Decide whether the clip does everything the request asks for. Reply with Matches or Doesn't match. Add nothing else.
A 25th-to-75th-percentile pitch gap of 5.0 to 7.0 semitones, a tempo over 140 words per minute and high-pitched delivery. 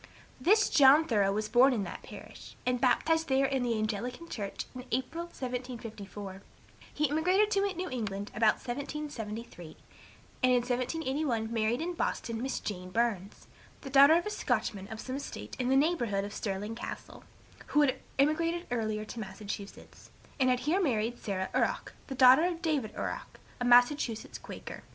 Matches